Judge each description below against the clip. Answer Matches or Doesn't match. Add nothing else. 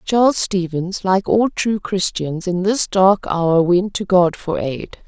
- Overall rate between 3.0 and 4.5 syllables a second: Matches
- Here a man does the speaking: Doesn't match